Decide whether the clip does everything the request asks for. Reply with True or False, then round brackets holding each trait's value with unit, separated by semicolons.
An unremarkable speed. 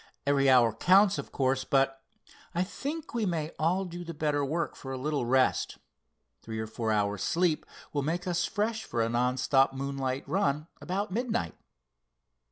True (175 wpm)